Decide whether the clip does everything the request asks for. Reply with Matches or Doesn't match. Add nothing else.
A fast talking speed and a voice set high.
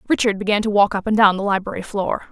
Matches